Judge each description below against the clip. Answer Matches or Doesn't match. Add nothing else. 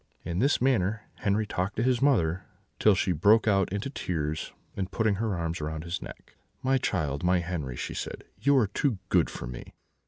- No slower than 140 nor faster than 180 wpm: Doesn't match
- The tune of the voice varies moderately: Matches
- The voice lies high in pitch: Doesn't match